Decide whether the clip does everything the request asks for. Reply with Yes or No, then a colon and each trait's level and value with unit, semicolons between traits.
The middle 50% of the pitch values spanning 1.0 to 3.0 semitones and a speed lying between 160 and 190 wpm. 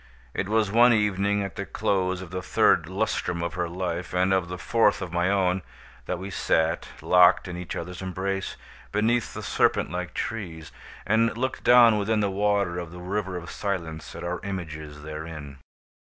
Yes: average, 2.7 semitones; average, 180 wpm